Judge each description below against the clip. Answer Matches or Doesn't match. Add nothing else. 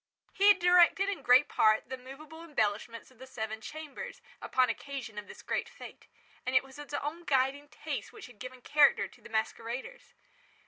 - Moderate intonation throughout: Matches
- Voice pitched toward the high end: Matches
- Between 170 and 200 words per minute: Matches